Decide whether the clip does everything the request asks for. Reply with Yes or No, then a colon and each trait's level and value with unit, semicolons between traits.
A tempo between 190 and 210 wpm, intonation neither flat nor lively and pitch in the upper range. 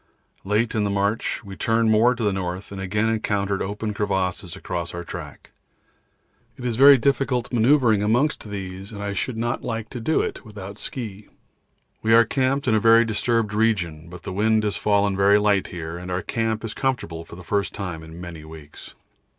No: average, 195 wpm; average, 3.2 semitones; low, 105 Hz